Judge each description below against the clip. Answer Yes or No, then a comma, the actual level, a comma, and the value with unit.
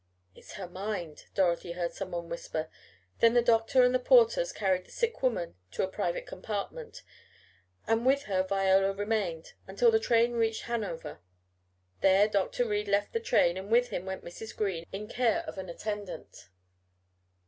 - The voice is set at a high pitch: Yes, high, 205 Hz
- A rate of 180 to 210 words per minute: No, average, 170 wpm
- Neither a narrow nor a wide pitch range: Yes, average, 4.2 semitones